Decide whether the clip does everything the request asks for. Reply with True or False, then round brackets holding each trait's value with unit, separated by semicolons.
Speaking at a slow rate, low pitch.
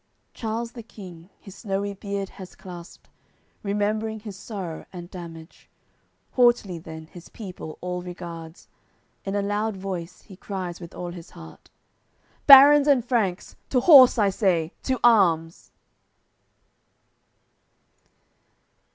False (120 wpm; 195 Hz)